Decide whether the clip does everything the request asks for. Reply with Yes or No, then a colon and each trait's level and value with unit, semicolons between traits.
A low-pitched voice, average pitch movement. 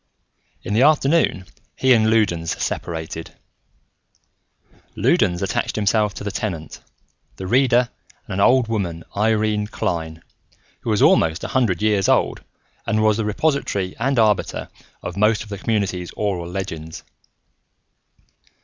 Yes: low, 105 Hz; average, 3.6 semitones